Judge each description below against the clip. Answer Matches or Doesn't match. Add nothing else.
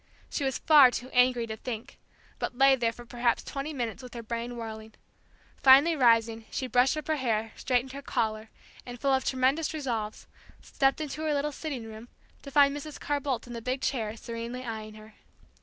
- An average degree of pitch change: Matches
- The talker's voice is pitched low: Doesn't match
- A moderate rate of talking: Matches